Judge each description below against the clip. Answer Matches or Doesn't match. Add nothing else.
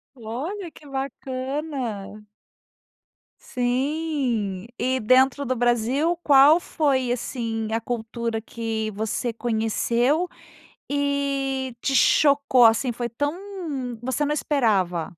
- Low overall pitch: Doesn't match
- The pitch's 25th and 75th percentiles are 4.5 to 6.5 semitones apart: Doesn't match